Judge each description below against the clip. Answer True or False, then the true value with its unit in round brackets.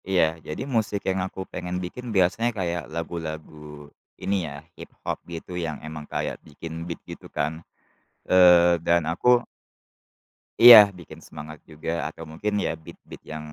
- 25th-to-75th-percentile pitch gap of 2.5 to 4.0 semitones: True (3.0 semitones)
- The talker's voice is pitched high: False (85 Hz)